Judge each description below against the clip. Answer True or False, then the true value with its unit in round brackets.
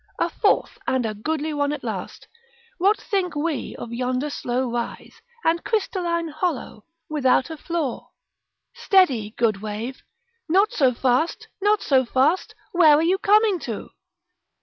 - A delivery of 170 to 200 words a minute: False (145 wpm)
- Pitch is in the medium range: False (295 Hz)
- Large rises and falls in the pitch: True (5.7 semitones)